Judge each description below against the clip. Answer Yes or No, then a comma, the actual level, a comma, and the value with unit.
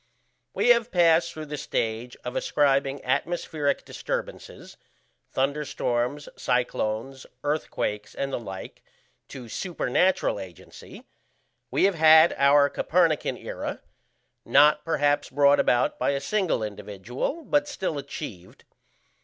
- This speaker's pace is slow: Yes, slow, 110 wpm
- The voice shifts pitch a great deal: No, average, 4.6 semitones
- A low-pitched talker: No, medium, 145 Hz